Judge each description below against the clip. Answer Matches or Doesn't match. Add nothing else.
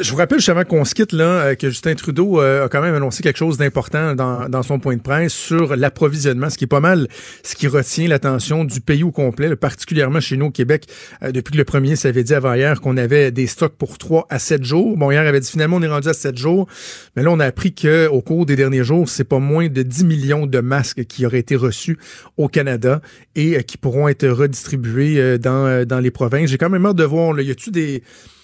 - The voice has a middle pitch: Matches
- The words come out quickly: Matches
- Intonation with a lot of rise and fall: Doesn't match